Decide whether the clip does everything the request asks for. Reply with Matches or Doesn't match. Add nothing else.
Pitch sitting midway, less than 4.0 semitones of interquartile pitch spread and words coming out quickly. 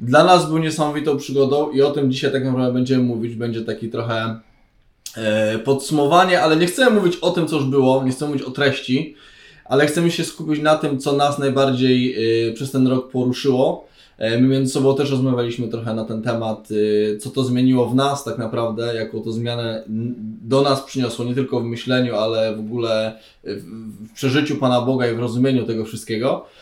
Doesn't match